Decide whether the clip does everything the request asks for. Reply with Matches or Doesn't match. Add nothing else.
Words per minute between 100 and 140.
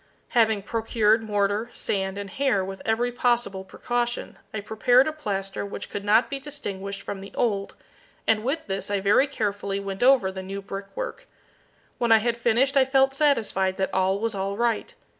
Doesn't match